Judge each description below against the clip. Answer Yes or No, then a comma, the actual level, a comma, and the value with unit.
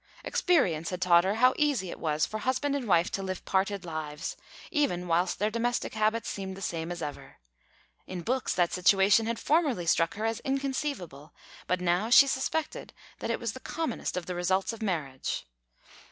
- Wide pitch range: Yes, wide, 5.7 semitones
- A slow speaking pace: No, average, 185 wpm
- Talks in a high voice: Yes, high, 195 Hz